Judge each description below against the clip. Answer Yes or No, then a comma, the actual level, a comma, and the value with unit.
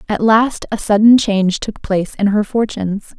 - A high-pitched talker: Yes, high, 210 Hz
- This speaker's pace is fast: No, average, 190 wpm